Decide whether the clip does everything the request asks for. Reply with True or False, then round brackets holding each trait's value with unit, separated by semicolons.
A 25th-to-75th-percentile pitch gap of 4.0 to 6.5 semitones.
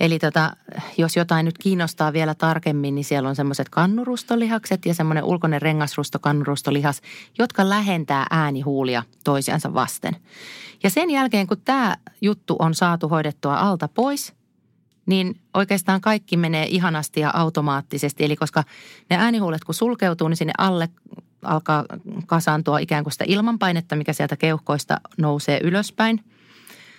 True (4.4 semitones)